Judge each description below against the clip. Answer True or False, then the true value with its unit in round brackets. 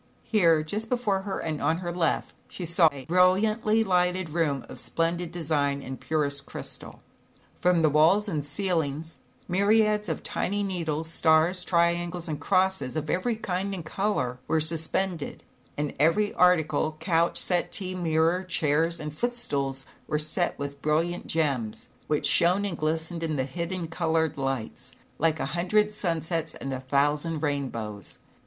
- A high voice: False (165 Hz)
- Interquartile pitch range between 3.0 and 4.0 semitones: True (3.4 semitones)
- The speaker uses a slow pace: False (150 wpm)